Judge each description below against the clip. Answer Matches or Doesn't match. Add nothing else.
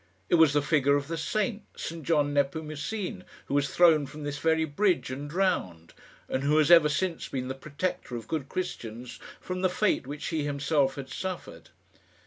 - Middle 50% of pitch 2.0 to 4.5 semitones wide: Matches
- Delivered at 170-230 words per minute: Matches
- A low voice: Doesn't match